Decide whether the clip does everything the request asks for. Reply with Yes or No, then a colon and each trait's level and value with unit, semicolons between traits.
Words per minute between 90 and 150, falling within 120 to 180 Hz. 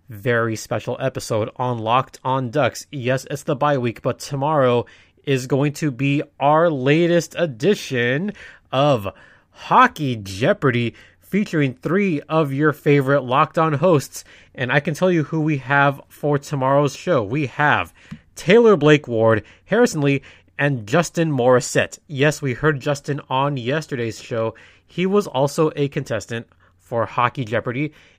Yes: average, 145 wpm; medium, 140 Hz